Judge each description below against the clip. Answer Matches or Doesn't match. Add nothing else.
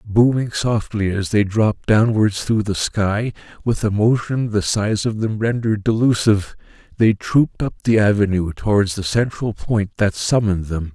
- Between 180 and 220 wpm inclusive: Doesn't match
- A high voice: Doesn't match